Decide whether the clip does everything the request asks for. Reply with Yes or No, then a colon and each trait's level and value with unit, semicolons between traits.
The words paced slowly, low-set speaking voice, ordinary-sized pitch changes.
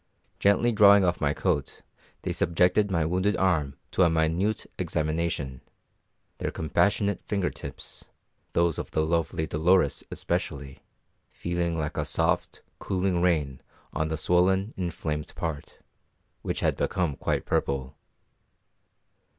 Yes: slow, 125 wpm; very low, 85 Hz; average, 3.4 semitones